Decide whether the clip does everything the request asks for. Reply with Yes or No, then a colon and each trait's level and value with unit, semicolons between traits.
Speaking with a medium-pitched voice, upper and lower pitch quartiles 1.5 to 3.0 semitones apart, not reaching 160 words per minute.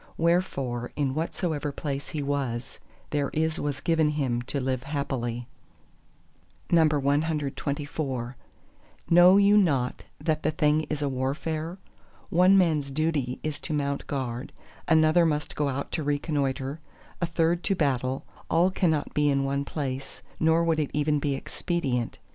Yes: medium, 145 Hz; average, 2.7 semitones; average, 140 wpm